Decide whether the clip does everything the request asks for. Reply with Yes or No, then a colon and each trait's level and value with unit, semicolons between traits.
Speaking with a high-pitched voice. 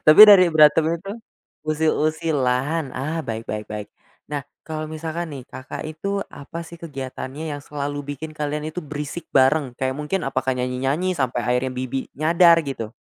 No: medium, 150 Hz